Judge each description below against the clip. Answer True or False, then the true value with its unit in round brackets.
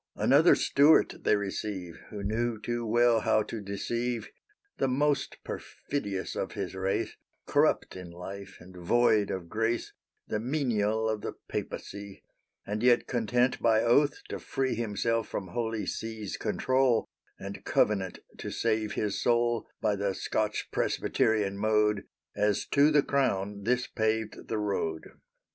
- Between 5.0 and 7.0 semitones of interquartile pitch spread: False (2.9 semitones)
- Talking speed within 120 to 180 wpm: True (140 wpm)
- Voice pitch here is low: True (110 Hz)